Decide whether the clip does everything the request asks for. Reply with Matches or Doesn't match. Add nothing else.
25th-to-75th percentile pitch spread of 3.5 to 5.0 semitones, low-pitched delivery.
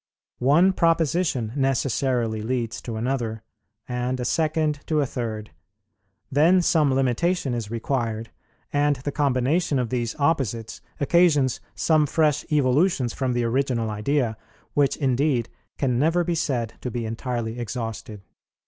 Matches